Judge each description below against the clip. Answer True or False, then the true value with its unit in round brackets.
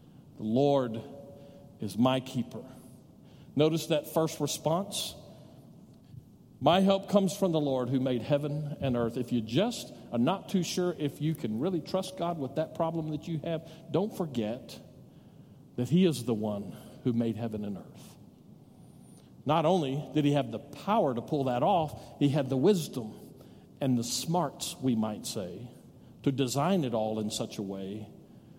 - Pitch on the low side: False (145 Hz)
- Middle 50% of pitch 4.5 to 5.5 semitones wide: True (5.1 semitones)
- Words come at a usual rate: True (170 wpm)